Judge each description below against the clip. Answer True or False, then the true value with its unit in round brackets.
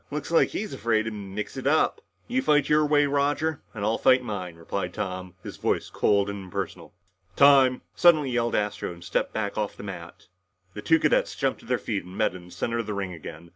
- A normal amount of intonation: False (6.6 semitones)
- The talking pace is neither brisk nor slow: False (220 wpm)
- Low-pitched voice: True (110 Hz)